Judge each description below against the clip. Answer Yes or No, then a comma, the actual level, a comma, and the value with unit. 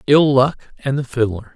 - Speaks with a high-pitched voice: No, low, 130 Hz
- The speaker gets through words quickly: No, average, 195 wpm